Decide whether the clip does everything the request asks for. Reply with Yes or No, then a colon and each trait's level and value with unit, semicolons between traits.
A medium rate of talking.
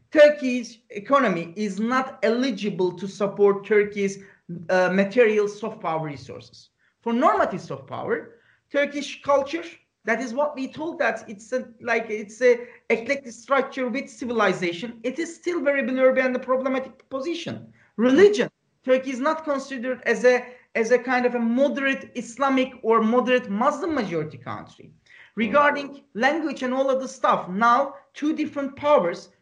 No: fast, 150 wpm